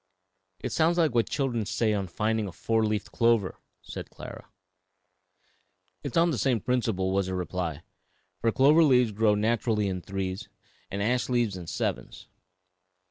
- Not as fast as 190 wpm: Yes, average, 165 wpm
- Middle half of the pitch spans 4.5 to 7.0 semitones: No, average, 4.0 semitones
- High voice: No, low, 110 Hz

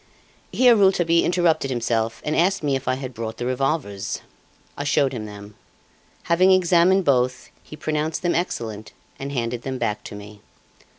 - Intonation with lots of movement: Yes, wide, 6.5 semitones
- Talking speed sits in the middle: Yes, average, 165 wpm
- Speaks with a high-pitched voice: No, low, 135 Hz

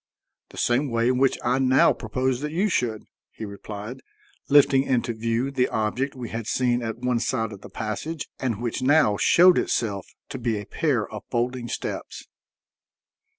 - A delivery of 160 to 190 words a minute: Yes, average, 175 wpm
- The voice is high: No, low, 125 Hz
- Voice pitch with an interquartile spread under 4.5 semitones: Yes, average, 3.0 semitones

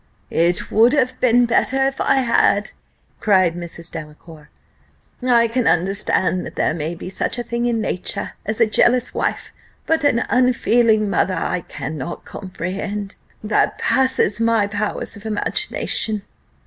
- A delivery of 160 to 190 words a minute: No, average, 145 wpm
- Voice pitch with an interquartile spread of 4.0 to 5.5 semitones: Yes, average, 4.6 semitones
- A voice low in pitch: No, high, 215 Hz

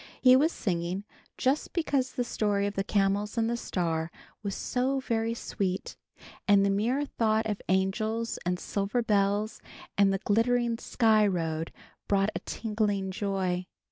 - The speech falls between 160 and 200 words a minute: No, average, 150 wpm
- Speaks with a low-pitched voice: No, high, 205 Hz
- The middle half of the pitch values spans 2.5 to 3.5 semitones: Yes, average, 2.9 semitones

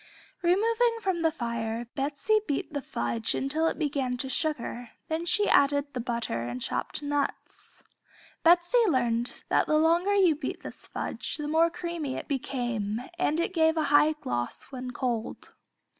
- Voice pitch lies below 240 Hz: No, very high, 290 Hz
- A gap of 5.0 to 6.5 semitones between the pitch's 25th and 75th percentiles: Yes, wide, 5.4 semitones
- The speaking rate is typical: Yes, average, 160 wpm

